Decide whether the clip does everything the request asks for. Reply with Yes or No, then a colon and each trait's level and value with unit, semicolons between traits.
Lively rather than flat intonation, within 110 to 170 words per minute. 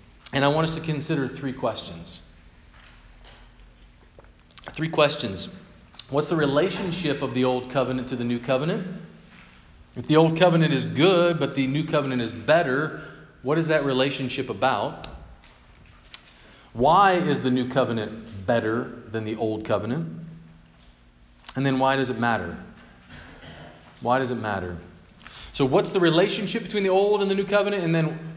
Yes: wide, 6.6 semitones; average, 150 wpm